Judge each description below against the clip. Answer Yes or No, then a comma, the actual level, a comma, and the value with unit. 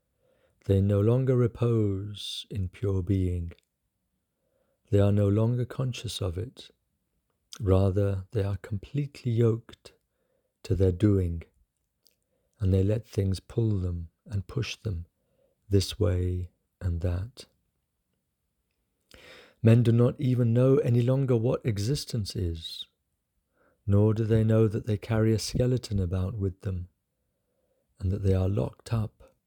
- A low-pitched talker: Yes, low, 100 Hz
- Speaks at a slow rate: Yes, slow, 130 wpm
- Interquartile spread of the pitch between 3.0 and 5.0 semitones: Yes, average, 3.7 semitones